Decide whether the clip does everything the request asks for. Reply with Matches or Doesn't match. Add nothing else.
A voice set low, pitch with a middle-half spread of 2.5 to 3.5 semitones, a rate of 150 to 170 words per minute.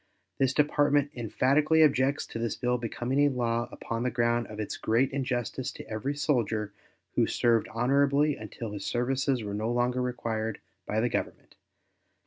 Matches